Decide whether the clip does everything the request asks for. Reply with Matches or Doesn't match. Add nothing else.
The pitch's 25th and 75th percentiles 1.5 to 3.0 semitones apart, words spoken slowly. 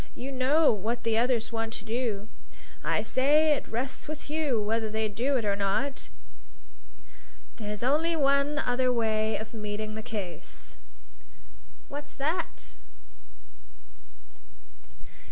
Doesn't match